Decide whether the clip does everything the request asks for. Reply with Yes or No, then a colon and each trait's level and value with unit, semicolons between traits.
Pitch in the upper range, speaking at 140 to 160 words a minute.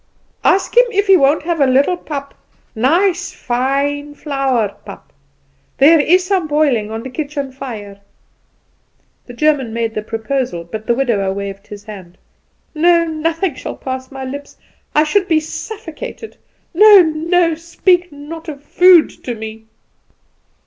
Yes: very high, 285 Hz; average, 145 wpm